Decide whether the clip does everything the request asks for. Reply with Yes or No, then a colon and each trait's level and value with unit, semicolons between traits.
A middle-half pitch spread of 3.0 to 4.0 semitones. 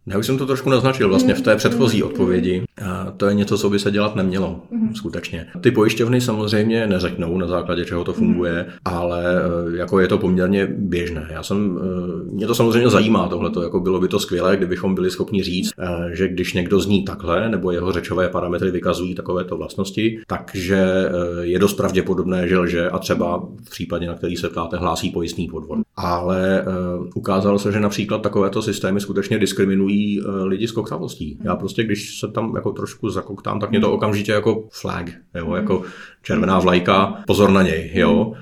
No: narrow, 2.5 semitones